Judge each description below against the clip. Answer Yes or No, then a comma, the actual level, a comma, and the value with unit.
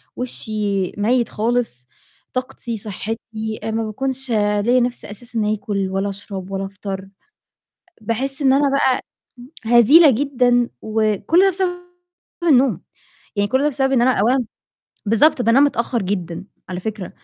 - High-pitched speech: Yes, high, 225 Hz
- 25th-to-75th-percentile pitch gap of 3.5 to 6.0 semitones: Yes, average, 4.1 semitones